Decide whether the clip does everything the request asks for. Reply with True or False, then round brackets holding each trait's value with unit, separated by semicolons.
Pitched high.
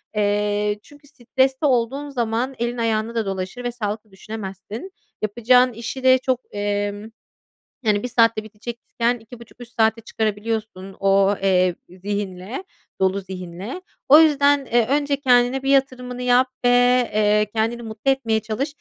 True (230 Hz)